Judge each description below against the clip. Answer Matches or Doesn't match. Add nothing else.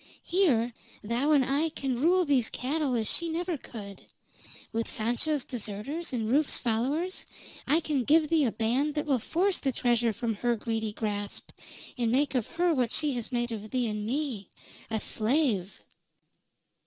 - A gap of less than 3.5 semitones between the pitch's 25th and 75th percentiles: Doesn't match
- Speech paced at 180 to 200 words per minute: Doesn't match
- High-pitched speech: Matches